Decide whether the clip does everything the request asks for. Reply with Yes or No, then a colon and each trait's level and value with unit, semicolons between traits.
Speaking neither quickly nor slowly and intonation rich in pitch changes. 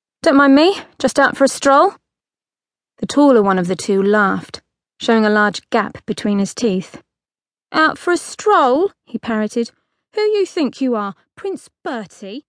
Yes: average, 170 wpm; wide, 7.2 semitones